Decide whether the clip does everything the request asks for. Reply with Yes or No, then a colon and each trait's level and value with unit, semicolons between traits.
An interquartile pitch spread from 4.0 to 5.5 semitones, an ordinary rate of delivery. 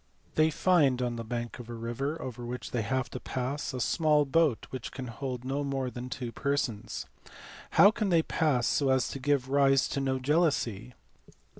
No: average, 2.8 semitones; average, 190 wpm